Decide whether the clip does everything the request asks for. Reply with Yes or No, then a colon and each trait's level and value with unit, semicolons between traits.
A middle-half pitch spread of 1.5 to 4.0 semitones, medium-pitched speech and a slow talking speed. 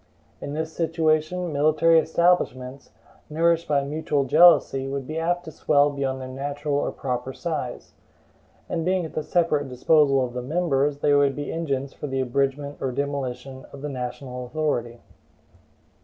No: average, 3.0 semitones; medium, 145 Hz; average, 155 wpm